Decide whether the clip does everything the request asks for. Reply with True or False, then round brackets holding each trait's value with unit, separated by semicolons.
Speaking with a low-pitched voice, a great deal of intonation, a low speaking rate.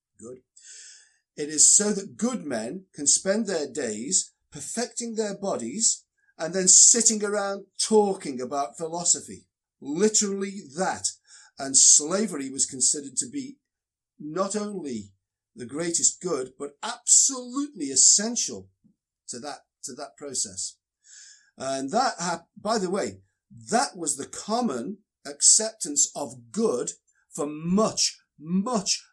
False (190 Hz; 7.7 semitones; 120 wpm)